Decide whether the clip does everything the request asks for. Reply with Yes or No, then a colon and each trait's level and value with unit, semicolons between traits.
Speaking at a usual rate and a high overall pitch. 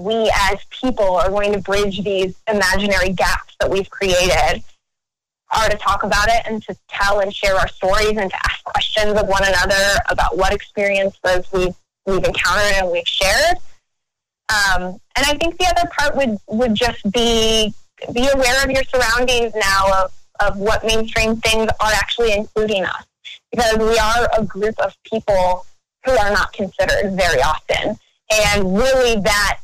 Yes: average, 170 wpm; high, 210 Hz